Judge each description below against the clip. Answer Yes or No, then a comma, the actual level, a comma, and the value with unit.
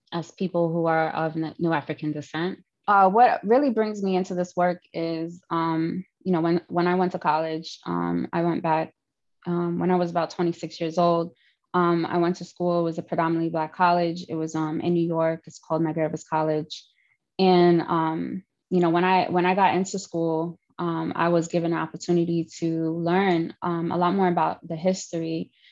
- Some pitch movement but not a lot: No, narrow, 1.6 semitones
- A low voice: No, medium, 170 Hz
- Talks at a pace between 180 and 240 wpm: Yes, average, 200 wpm